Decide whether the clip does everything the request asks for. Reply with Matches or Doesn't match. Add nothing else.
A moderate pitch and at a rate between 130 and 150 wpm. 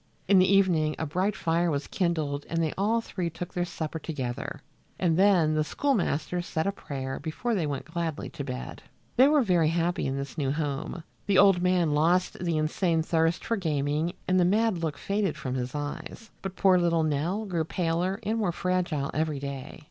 Doesn't match